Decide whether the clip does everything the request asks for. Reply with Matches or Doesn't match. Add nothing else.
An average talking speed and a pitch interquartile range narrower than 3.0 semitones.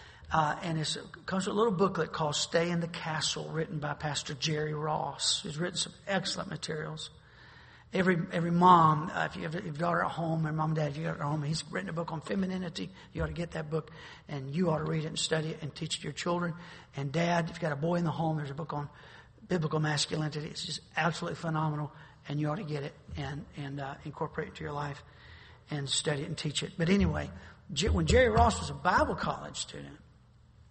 Doesn't match